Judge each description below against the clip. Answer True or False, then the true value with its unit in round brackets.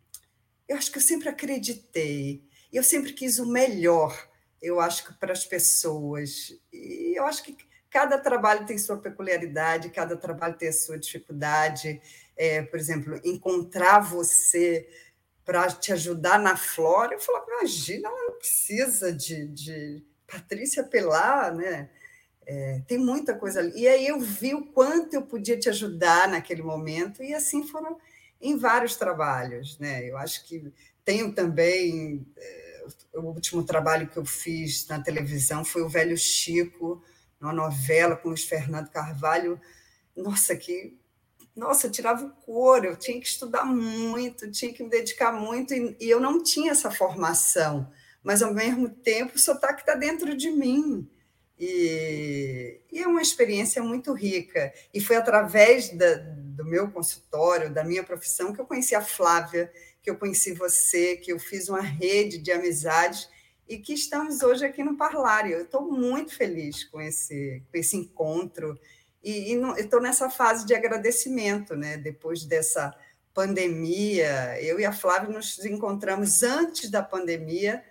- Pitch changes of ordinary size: False (7.5 semitones)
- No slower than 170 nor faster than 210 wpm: False (155 wpm)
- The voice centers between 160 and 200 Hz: True (190 Hz)